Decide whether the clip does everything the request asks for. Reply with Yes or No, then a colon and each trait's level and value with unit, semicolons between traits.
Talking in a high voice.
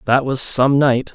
No: low, 130 Hz